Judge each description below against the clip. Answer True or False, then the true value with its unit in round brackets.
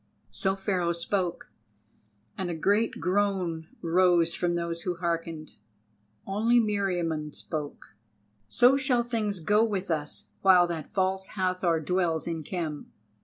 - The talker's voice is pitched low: False (180 Hz)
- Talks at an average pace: False (125 wpm)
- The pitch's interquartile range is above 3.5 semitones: False (3.0 semitones)